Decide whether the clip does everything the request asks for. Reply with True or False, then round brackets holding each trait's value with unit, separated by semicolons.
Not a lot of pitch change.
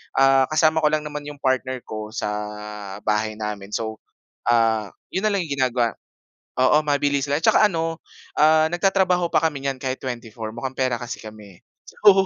False (5.1 semitones)